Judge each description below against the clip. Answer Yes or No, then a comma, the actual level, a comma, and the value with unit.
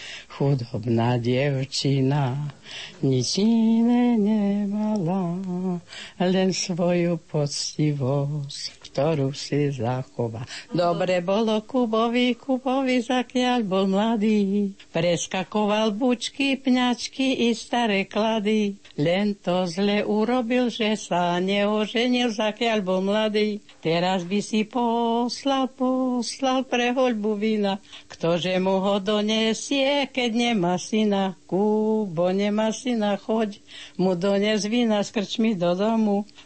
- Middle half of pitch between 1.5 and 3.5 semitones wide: No, average, 4.7 semitones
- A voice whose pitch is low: No, high, 205 Hz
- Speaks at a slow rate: Yes, slow, 95 wpm